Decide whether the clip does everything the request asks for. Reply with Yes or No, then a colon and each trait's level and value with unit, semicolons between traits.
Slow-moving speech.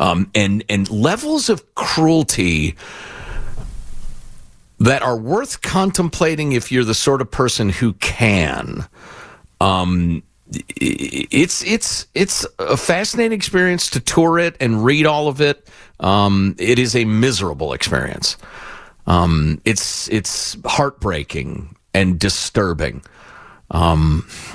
Yes: slow, 110 wpm